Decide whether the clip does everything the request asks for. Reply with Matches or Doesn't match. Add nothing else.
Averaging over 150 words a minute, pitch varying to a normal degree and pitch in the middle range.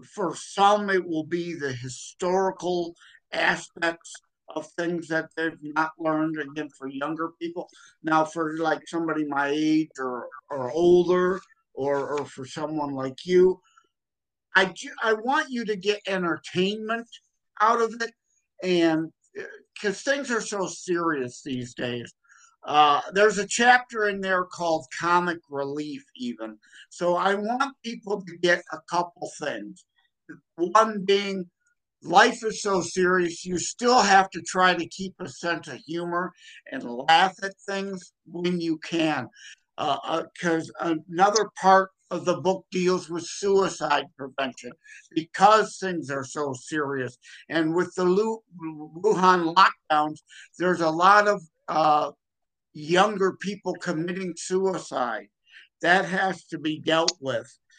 Doesn't match